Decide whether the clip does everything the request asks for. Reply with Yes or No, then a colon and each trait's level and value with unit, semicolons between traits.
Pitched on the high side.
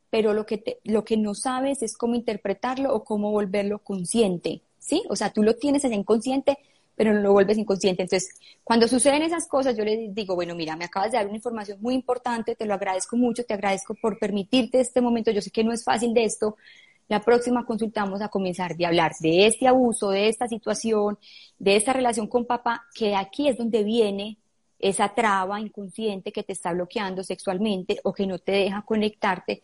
Yes: high, 215 Hz